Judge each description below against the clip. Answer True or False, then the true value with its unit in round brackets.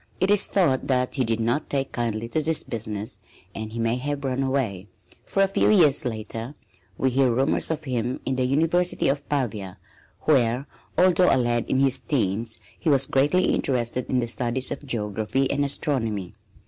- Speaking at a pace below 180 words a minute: False (185 wpm)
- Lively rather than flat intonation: False (3.7 semitones)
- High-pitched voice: False (130 Hz)